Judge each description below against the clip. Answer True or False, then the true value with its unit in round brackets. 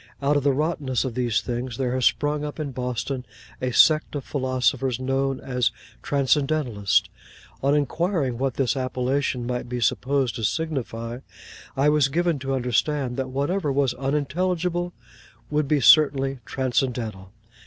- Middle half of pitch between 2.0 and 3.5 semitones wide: True (2.7 semitones)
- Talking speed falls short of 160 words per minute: True (145 wpm)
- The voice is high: False (135 Hz)